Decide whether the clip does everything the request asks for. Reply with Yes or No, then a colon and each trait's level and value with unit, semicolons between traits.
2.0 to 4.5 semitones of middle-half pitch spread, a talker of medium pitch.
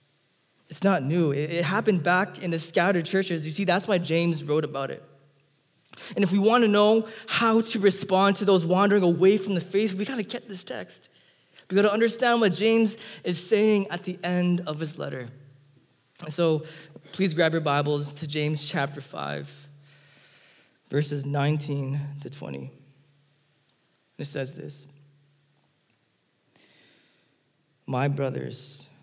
No: average, 5.2 semitones; medium, 160 Hz